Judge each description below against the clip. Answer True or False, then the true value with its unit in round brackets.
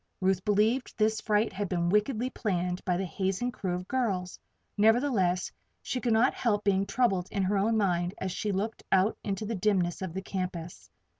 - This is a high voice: True (195 Hz)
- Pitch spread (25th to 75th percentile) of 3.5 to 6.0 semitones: False (3.1 semitones)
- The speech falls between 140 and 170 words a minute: False (190 wpm)